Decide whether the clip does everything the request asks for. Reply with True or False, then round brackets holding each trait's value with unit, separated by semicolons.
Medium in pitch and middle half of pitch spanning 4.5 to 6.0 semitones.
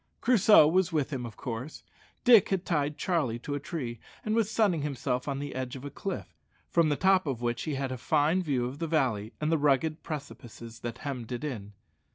True (145 Hz; 4.9 semitones)